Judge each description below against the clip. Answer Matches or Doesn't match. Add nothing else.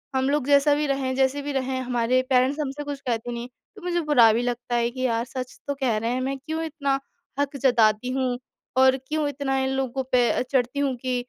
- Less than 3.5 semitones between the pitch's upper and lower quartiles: Matches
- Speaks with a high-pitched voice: Matches